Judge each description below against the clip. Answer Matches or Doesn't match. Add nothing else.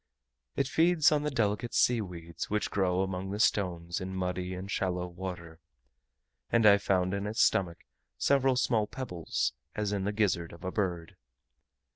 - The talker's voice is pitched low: Matches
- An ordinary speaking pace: Matches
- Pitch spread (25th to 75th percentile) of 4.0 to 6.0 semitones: Doesn't match